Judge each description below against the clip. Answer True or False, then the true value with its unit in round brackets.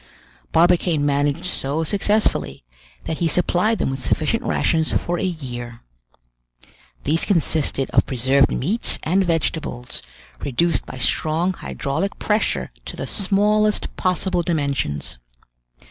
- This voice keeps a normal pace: False (115 wpm)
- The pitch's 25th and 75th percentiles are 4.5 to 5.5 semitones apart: True (4.9 semitones)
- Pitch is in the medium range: True (165 Hz)